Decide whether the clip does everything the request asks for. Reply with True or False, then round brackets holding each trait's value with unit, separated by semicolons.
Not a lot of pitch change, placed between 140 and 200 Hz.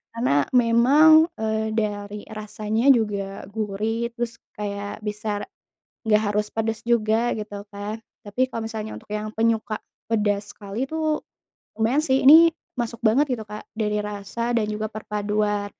False (2.0 semitones; 215 Hz)